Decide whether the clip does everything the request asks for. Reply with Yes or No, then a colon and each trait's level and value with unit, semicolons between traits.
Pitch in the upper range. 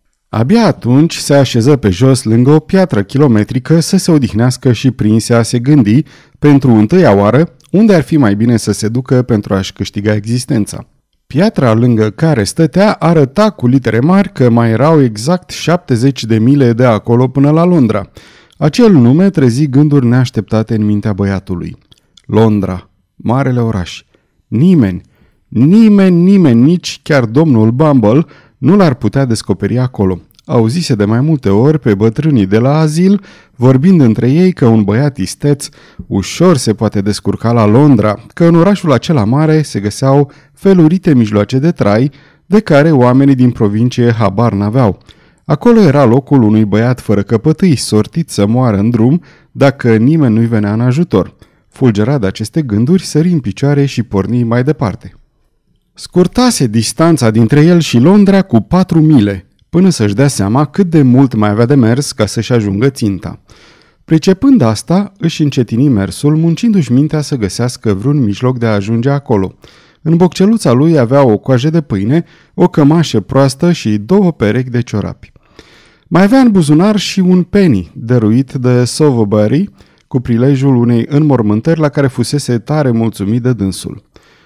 No: low, 130 Hz